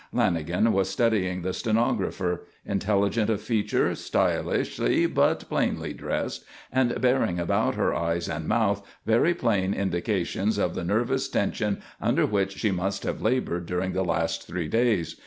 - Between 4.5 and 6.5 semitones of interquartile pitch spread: No, average, 3.8 semitones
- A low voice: Yes, low, 100 Hz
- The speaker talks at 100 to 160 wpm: Yes, average, 145 wpm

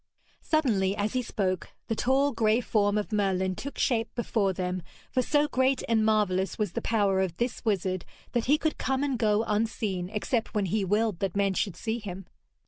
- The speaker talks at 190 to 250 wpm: Yes, average, 195 wpm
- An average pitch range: Yes, average, 3.8 semitones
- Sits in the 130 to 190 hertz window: No, high, 215 Hz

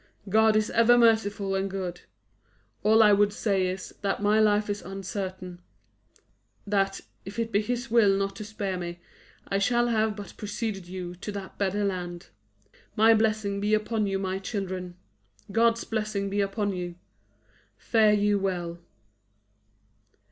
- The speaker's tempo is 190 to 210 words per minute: No, average, 150 wpm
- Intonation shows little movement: Yes, narrow, 2.1 semitones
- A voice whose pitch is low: No, high, 205 Hz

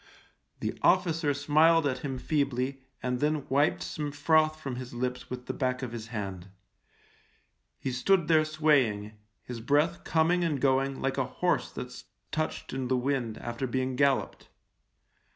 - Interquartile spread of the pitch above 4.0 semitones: No, average, 3.6 semitones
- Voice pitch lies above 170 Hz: No, low, 135 Hz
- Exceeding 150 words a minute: Yes, average, 160 wpm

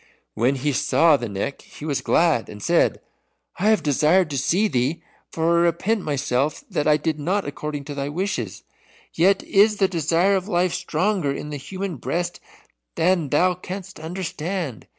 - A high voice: No, medium, 160 Hz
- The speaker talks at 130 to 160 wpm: No, average, 170 wpm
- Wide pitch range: No, average, 4.5 semitones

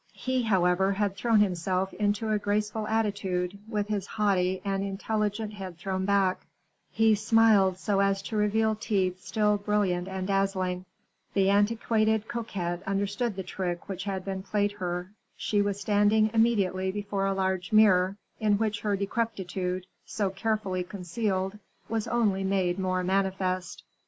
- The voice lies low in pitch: No, high, 200 Hz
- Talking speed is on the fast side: No, average, 145 wpm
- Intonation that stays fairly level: Yes, narrow, 2.0 semitones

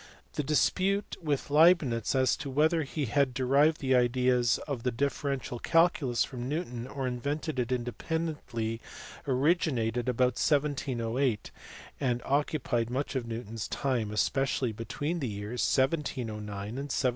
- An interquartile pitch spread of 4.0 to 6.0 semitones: No, average, 3.4 semitones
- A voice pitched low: Yes, low, 130 Hz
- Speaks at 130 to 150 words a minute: Yes, slow, 135 wpm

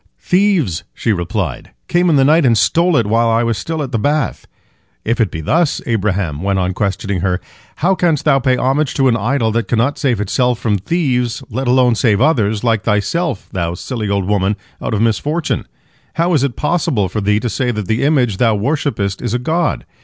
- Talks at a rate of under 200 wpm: No, fast, 205 wpm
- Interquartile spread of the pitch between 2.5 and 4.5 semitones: No, wide, 5.6 semitones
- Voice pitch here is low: Yes, low, 115 Hz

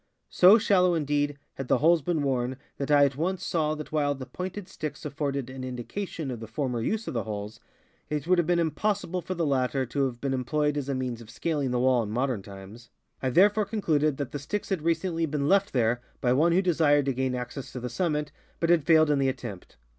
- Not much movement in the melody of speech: No, average, 4.7 semitones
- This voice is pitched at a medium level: Yes, medium, 145 Hz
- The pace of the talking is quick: Yes, fast, 235 wpm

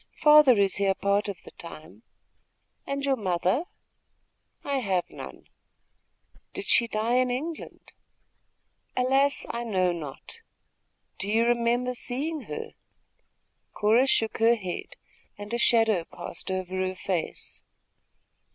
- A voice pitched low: No, high, 225 Hz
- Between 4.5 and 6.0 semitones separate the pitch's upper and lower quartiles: Yes, average, 5.1 semitones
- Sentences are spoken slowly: Yes, slow, 125 wpm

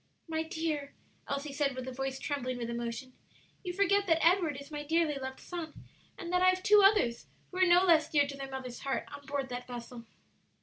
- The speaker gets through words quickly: Yes, fast, 215 wpm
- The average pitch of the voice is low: No, very high, 285 Hz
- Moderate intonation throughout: Yes, average, 4.6 semitones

